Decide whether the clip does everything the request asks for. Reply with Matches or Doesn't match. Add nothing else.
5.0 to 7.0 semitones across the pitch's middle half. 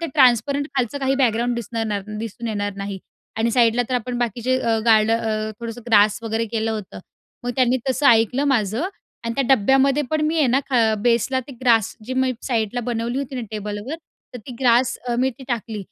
Doesn't match